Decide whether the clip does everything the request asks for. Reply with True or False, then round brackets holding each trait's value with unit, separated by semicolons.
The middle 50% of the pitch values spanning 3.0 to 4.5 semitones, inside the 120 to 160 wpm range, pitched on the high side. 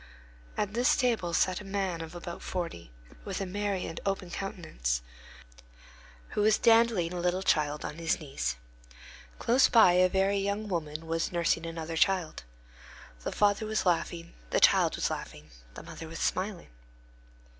False (3.5 semitones; 155 wpm; 180 Hz)